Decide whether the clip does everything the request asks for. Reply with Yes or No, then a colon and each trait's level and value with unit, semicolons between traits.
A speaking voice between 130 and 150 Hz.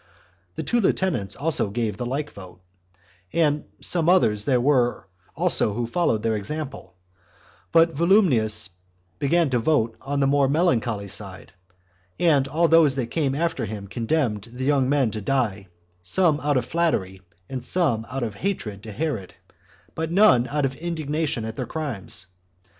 Yes: low, 135 Hz